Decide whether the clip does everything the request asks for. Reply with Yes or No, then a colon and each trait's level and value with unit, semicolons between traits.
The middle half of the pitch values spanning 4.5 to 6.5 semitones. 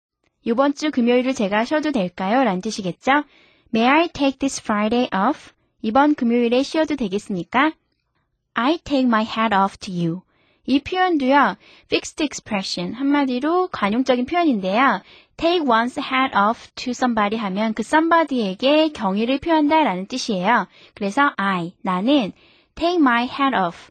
Yes: wide, 5.4 semitones